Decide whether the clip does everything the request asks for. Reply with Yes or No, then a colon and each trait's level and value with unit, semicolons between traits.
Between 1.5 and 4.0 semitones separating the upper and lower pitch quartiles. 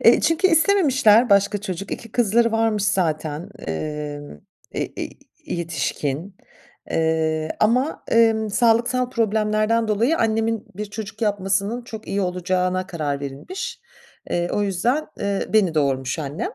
No: average, 5.1 semitones